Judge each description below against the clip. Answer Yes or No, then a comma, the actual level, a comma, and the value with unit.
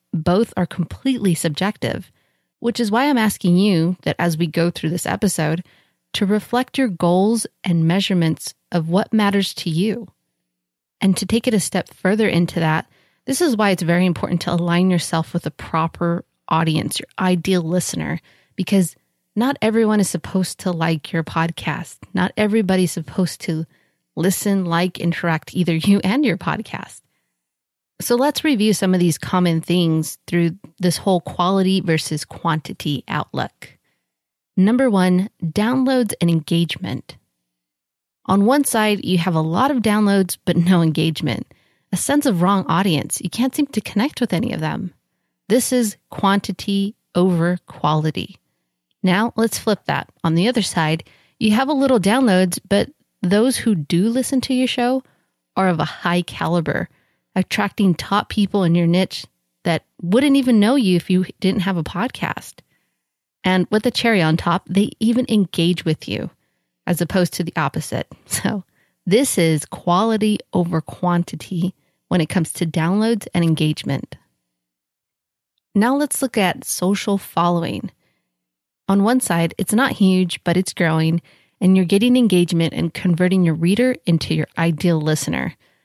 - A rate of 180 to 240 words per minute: No, average, 155 wpm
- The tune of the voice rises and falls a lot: No, average, 4.1 semitones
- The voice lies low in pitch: No, medium, 180 Hz